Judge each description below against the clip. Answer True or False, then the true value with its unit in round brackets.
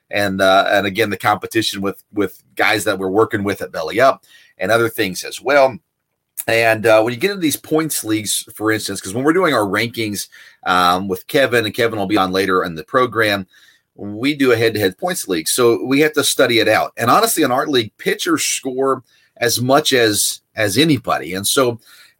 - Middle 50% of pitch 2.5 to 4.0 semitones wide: False (4.7 semitones)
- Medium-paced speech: False (215 wpm)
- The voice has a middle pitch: False (110 Hz)